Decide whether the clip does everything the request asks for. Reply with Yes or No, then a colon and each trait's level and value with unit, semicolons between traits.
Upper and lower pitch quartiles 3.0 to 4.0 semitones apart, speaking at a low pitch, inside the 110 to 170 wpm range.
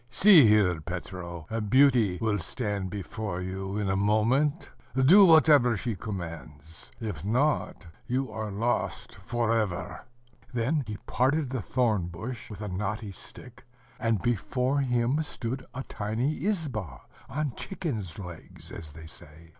No: average, 5.3 semitones; low, 110 Hz; average, 140 wpm